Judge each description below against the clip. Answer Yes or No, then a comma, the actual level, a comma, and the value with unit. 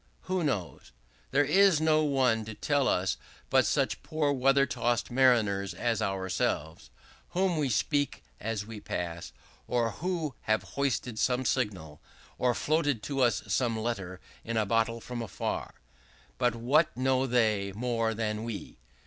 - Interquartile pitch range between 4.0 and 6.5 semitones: Yes, average, 4.6 semitones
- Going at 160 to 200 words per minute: No, average, 150 wpm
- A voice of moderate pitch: No, low, 120 Hz